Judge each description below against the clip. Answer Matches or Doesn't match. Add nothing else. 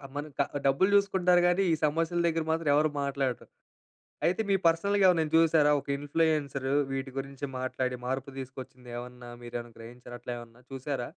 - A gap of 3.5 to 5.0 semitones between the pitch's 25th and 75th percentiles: Matches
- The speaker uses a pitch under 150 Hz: Matches